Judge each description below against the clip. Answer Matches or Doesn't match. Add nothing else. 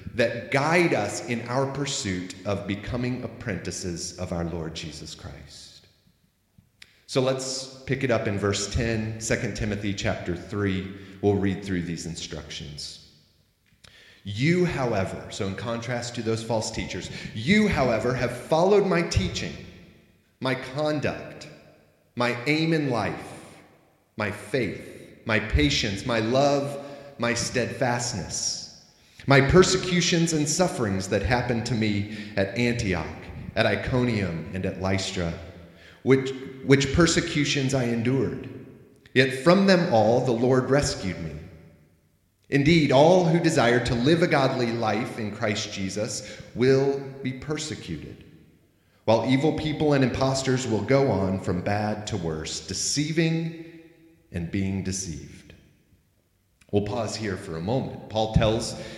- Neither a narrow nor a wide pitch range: Doesn't match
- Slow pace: Matches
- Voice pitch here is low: Matches